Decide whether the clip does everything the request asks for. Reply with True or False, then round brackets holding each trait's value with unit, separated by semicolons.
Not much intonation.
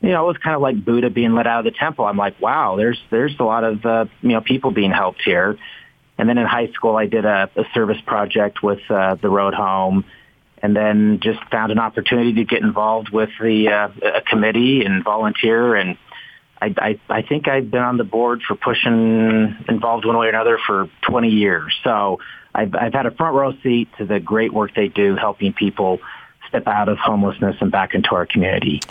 True (2.2 semitones)